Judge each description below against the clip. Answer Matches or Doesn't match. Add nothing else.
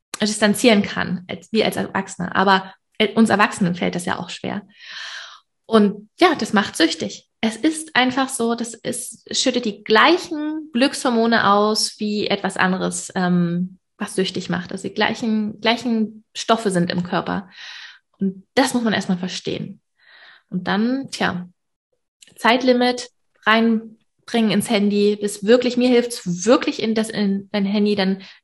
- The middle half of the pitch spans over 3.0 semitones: Matches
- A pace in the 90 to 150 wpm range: Matches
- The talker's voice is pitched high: Matches